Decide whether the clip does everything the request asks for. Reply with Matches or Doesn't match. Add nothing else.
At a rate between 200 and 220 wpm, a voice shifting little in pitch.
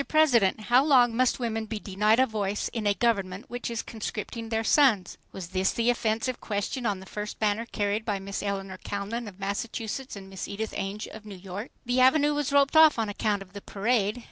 Doesn't match